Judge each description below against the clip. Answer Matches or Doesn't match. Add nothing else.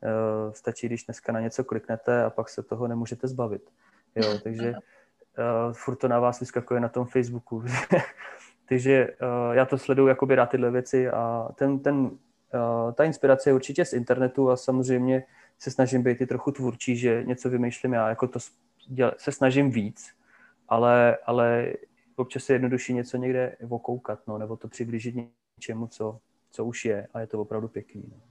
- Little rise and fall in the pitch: Matches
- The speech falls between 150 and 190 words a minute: Matches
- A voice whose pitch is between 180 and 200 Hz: Doesn't match